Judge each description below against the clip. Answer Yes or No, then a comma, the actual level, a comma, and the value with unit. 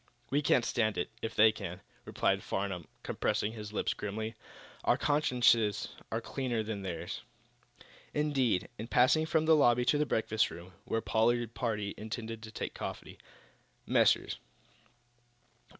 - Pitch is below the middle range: Yes, low, 110 Hz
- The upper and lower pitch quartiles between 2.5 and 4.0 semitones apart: Yes, average, 2.9 semitones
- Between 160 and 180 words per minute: No, average, 145 wpm